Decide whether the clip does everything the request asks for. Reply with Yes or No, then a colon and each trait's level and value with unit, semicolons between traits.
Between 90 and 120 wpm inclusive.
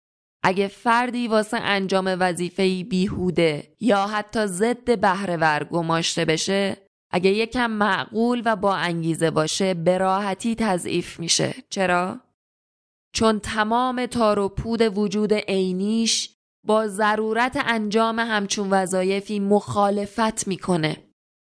Yes: slow, 105 wpm